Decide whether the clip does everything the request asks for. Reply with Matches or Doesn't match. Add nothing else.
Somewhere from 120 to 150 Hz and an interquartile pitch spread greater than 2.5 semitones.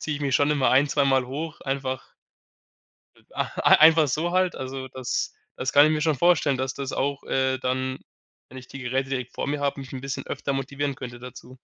Doesn't match